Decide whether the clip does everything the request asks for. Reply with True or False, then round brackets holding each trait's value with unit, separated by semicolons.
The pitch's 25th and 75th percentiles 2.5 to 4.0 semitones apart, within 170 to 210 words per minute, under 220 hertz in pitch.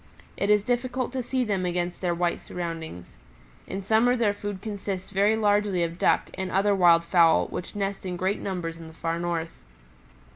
True (3.2 semitones; 185 wpm; 190 Hz)